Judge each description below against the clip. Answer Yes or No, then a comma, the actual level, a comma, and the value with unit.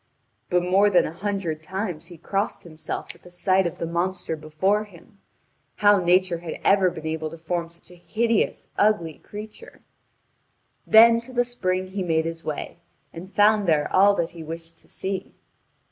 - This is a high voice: No, medium, 180 Hz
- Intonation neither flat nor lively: Yes, average, 3.5 semitones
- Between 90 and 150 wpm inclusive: No, average, 175 wpm